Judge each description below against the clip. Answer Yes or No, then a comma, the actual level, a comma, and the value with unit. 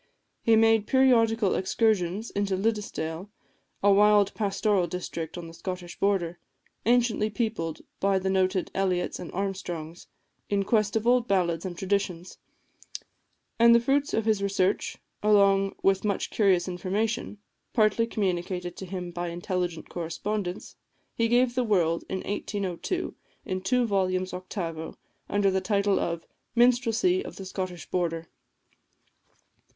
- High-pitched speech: Yes, high, 195 Hz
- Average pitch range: Yes, average, 3.3 semitones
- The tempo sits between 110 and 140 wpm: Yes, slow, 135 wpm